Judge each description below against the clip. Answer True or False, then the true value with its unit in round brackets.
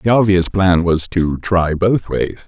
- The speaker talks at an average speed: True (195 wpm)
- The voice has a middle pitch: False (90 Hz)